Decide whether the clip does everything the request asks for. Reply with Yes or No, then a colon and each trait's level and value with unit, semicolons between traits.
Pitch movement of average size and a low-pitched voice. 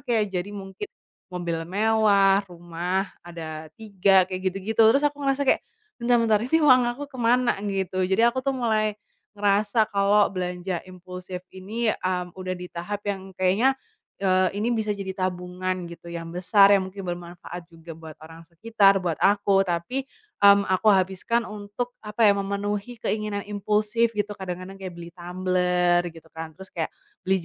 No: average, 3.0 semitones; high, 195 Hz